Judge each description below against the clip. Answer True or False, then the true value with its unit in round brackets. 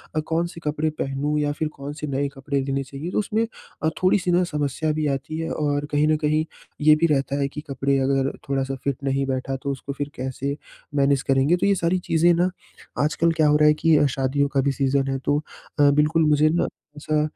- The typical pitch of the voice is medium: True (145 Hz)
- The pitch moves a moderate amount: False (2.2 semitones)